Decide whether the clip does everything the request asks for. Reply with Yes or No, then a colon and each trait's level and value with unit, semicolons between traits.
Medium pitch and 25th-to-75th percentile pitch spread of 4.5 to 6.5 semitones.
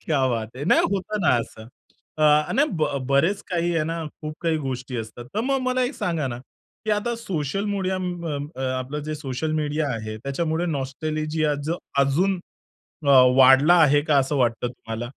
Yes: medium, 155 Hz; average, 4.8 semitones